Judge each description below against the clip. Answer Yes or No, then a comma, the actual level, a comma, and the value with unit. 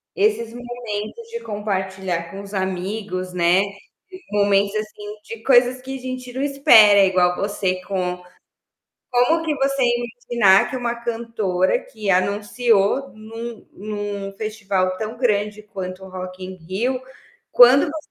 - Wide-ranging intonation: No, average, 4.2 semitones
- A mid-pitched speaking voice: No, high, 210 Hz